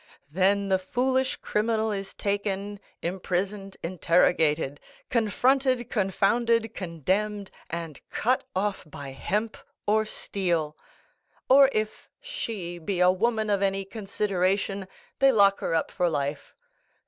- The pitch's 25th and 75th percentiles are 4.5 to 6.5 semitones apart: No, average, 3.3 semitones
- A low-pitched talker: No, high, 200 Hz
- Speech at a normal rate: No, slow, 115 wpm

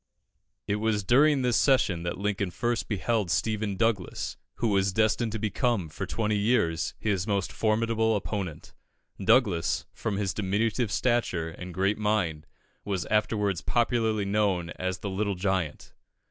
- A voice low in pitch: Yes, low, 105 Hz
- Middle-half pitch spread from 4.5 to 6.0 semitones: No, average, 3.1 semitones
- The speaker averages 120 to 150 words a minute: Yes, average, 145 wpm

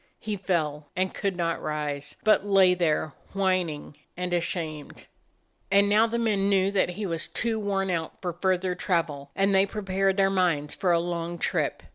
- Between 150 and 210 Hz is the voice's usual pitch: Yes, medium, 185 Hz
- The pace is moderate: Yes, average, 175 wpm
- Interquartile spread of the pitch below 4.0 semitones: Yes, average, 2.8 semitones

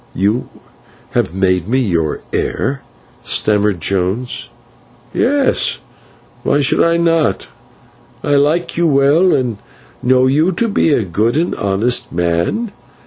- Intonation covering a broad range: Yes, wide, 8.4 semitones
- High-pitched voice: No, low, 130 Hz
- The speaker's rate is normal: No, slow, 125 wpm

